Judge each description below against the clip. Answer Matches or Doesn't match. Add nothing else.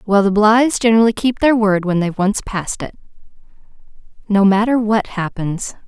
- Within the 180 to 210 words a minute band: Doesn't match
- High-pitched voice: Matches